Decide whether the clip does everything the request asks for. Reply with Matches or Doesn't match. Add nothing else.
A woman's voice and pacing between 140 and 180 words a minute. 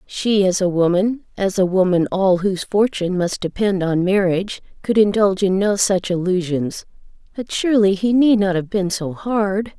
Matches